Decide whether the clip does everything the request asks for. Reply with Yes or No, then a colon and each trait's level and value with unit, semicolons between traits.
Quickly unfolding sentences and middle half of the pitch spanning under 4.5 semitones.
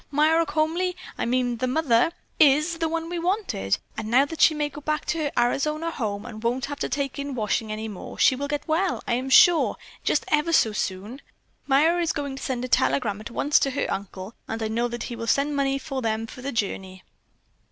No: fast, 225 wpm; average, 5.0 semitones